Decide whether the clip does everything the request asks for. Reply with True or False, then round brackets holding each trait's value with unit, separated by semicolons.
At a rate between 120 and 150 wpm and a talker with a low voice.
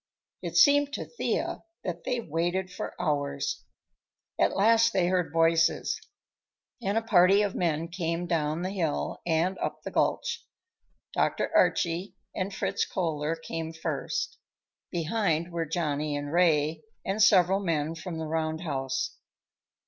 False (135 wpm; 170 Hz)